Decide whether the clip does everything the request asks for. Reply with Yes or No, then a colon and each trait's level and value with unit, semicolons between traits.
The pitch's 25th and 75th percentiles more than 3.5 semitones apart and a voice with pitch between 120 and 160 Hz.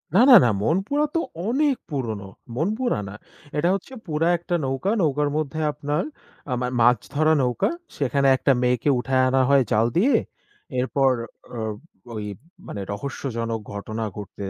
Yes: average, 5.3 semitones; medium, 140 Hz